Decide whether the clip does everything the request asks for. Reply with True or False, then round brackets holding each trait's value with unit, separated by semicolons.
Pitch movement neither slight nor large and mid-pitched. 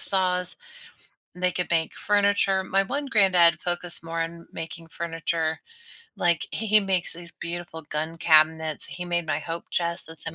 False (2.0 semitones; 170 Hz)